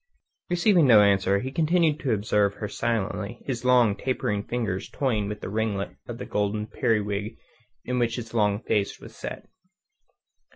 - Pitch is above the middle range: No, low, 110 Hz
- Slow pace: No, average, 160 wpm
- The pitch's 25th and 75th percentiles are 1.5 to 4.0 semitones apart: Yes, average, 3.5 semitones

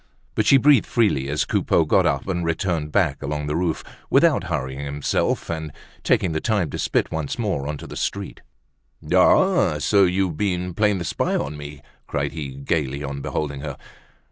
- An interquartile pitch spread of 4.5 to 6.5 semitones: Yes, average, 4.9 semitones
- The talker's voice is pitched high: No, very low, 80 Hz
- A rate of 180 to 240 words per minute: Yes, average, 185 wpm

